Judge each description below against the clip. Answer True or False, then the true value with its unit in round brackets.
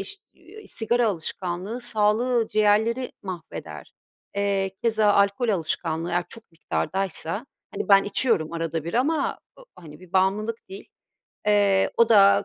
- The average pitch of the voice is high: True (200 Hz)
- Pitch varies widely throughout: False (3.9 semitones)